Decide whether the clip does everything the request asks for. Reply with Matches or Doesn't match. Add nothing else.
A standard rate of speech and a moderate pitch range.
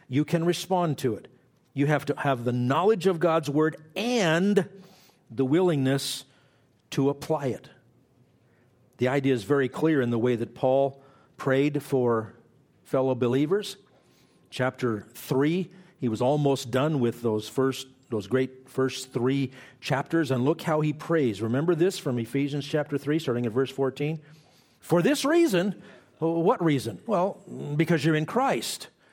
Matches